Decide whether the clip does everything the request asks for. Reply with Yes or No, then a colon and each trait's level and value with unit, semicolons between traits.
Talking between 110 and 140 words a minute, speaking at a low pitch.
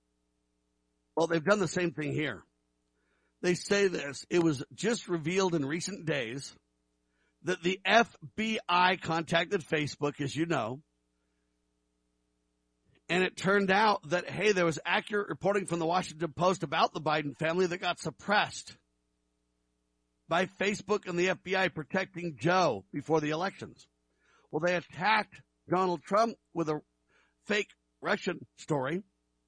No: slow, 135 wpm; medium, 160 Hz